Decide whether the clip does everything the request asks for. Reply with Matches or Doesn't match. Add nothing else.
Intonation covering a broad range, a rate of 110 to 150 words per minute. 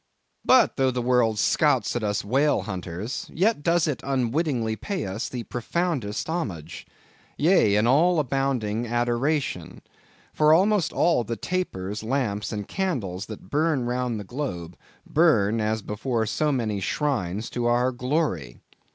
Matches